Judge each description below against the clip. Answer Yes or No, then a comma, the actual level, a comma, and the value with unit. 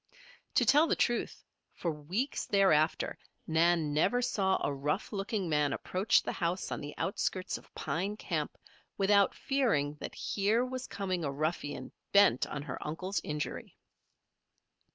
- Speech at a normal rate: Yes, average, 145 wpm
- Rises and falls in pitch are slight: No, average, 5.2 semitones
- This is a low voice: No, medium, 185 Hz